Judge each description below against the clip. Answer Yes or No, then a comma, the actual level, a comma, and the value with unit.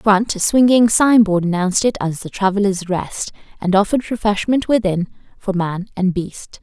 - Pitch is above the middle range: Yes, high, 200 Hz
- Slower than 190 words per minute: Yes, average, 180 wpm